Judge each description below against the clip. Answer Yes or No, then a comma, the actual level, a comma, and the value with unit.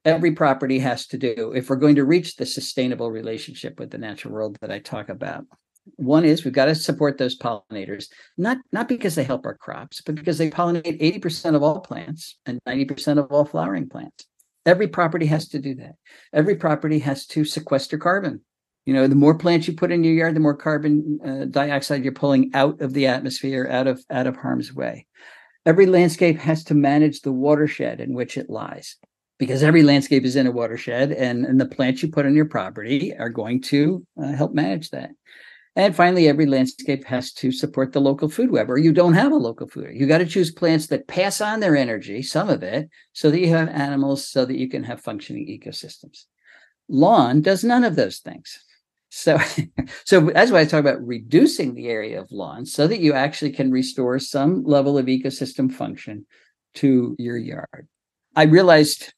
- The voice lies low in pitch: No, medium, 145 Hz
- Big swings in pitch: No, average, 3.3 semitones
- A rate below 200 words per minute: No, fast, 205 wpm